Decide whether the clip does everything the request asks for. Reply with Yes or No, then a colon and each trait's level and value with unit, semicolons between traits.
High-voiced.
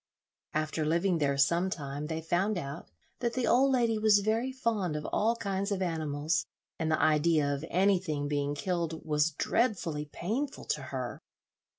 No: medium, 170 Hz